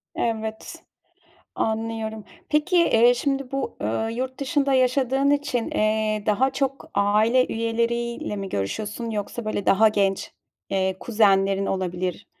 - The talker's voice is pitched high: Yes, high, 225 Hz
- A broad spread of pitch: No, average, 3.9 semitones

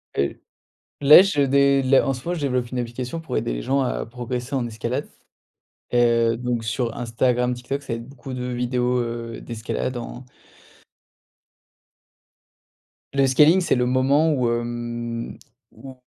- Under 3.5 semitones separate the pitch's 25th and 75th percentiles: Yes, narrow, 2.4 semitones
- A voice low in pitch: Yes, low, 125 Hz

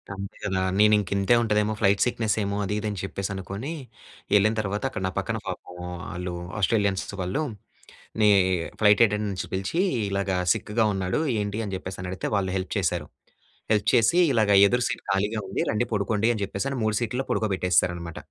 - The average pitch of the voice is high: No, low, 100 Hz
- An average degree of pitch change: No, narrow, 2.0 semitones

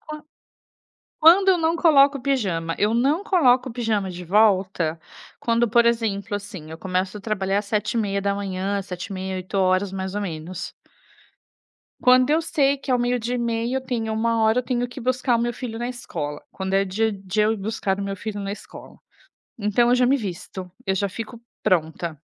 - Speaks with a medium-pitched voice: No, high, 215 Hz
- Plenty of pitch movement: No, average, 4.3 semitones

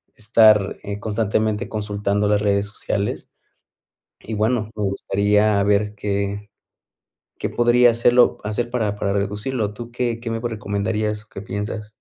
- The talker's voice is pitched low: Yes, low, 105 Hz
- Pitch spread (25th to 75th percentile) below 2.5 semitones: Yes, narrow, 1.8 semitones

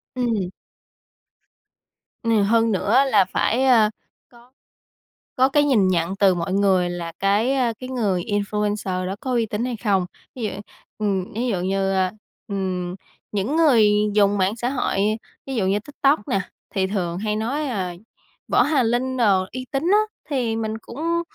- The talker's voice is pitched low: No, high, 215 Hz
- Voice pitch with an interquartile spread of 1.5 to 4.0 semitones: No, average, 4.5 semitones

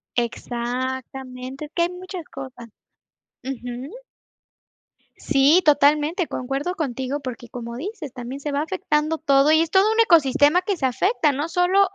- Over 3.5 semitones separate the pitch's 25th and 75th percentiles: Yes, average, 4.7 semitones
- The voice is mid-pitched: No, very high, 285 Hz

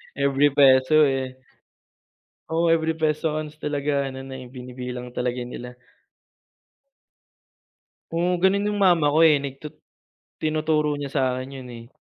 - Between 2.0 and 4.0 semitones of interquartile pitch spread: Yes, average, 3.0 semitones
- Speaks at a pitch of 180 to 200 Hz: No, medium, 140 Hz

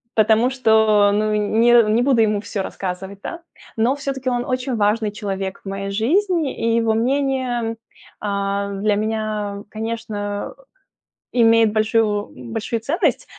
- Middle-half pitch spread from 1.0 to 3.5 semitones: Yes, average, 2.7 semitones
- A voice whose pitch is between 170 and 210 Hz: No, high, 220 Hz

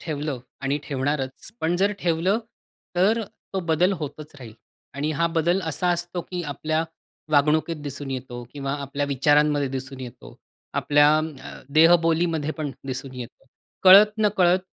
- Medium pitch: Yes, medium, 150 Hz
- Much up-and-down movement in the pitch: No, average, 3.8 semitones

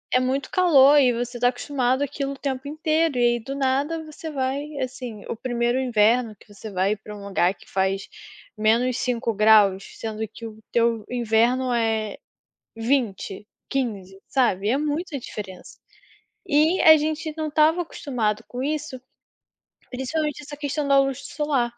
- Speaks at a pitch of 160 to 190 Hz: No, very high, 255 Hz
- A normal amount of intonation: Yes, average, 4.5 semitones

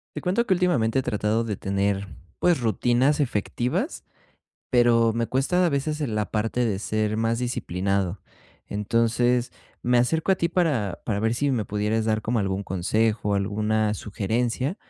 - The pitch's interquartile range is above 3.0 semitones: Yes, average, 3.5 semitones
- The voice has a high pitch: No, low, 115 Hz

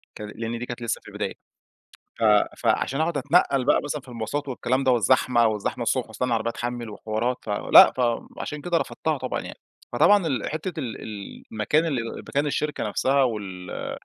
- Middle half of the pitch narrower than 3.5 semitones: No, average, 4.3 semitones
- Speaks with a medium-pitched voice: No, low, 125 Hz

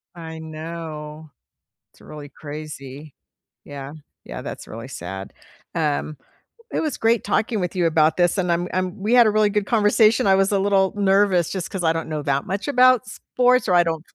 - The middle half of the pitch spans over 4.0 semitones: Yes, average, 4.9 semitones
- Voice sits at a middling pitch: Yes, medium, 175 Hz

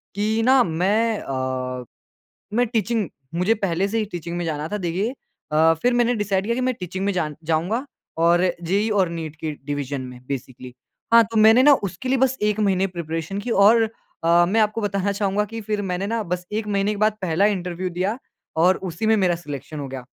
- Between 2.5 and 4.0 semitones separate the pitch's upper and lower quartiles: No, average, 4.9 semitones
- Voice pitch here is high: Yes, high, 195 Hz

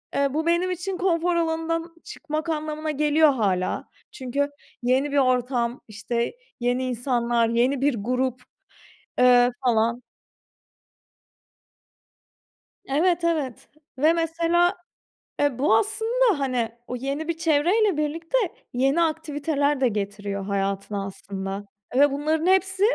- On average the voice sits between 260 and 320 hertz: Yes, very high, 285 Hz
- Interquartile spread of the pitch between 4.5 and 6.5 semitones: Yes, average, 5.2 semitones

